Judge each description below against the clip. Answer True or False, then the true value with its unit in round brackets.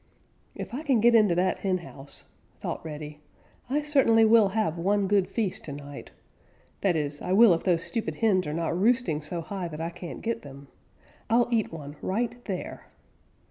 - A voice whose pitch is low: False (185 Hz)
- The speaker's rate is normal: True (180 wpm)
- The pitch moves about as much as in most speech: False (5.8 semitones)